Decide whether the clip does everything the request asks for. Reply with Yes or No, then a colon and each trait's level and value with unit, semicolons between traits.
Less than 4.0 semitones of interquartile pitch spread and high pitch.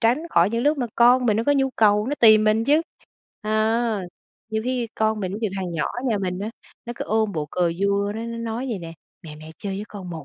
Yes: average, 3.1 semitones; high, 215 Hz